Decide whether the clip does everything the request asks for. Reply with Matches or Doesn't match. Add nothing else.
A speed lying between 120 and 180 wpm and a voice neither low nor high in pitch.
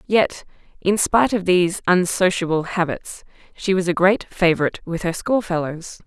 Matches